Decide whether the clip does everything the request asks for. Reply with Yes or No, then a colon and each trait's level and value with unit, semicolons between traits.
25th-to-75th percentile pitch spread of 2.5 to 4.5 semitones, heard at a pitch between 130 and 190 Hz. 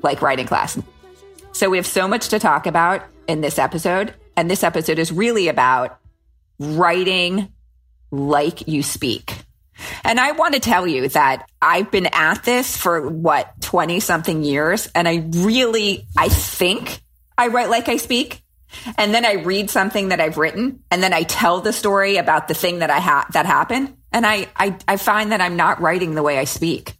No: wide, 5.4 semitones; medium, 185 Hz